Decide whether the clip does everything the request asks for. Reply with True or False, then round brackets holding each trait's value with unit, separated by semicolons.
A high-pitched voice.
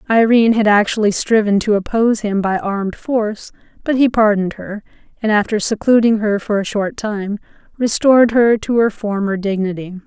True (215 Hz)